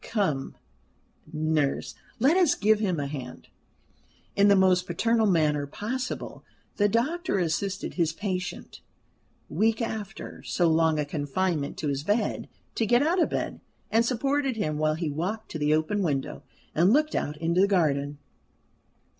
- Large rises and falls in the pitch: Yes, wide, 6.2 semitones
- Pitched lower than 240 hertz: Yes, medium, 185 Hz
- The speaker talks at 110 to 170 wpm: Yes, average, 155 wpm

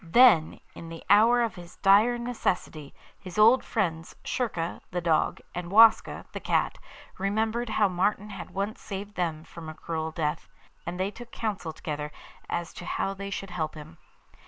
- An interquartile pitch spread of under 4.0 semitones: No, average, 4.6 semitones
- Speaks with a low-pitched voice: No, high, 190 Hz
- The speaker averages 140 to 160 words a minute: No, average, 170 wpm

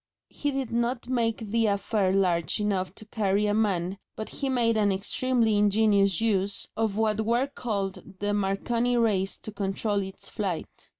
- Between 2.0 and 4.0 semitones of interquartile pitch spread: Yes, average, 2.7 semitones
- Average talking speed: Yes, average, 170 wpm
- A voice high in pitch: Yes, high, 210 Hz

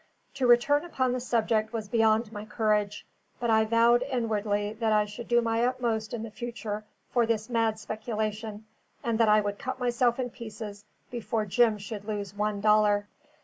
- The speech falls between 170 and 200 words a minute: Yes, average, 180 wpm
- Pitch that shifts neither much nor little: No, narrow, 2.1 semitones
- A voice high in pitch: Yes, high, 220 Hz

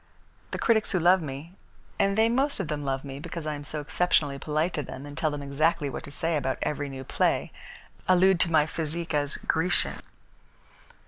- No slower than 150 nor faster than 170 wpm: No, average, 200 wpm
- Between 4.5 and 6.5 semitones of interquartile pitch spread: No, average, 3.4 semitones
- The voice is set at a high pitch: No, medium, 155 Hz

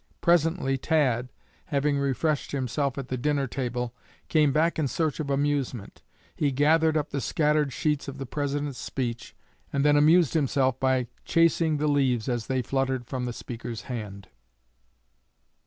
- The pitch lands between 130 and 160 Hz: Yes, medium, 140 Hz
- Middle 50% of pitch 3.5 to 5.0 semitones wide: No, average, 2.9 semitones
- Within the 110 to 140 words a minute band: No, average, 155 wpm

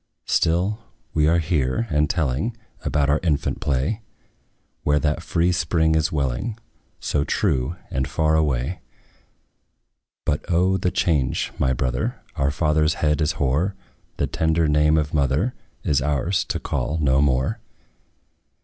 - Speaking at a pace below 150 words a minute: Yes, average, 140 wpm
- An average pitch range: Yes, average, 3.1 semitones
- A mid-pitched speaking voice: No, very low, 75 Hz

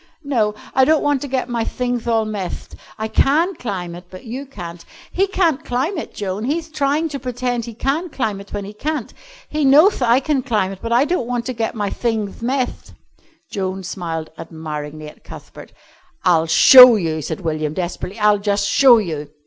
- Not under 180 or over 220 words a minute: Yes, average, 195 wpm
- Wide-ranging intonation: Yes, wide, 6.2 semitones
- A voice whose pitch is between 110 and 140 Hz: No, high, 230 Hz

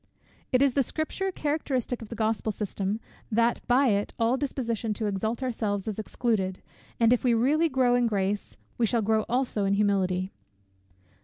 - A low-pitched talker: No, high, 230 Hz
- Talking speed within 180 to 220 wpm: No, average, 170 wpm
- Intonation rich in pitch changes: No, average, 3.5 semitones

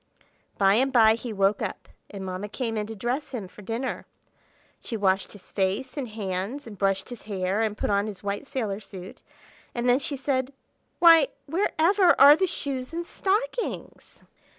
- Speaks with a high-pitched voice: Yes, high, 225 Hz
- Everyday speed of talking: Yes, average, 180 wpm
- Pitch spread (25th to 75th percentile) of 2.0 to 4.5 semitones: No, wide, 5.6 semitones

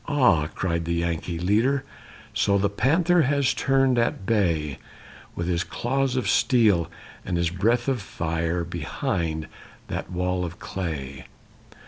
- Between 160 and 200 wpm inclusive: No, slow, 135 wpm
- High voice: No, very low, 95 Hz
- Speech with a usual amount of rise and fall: No, wide, 6.6 semitones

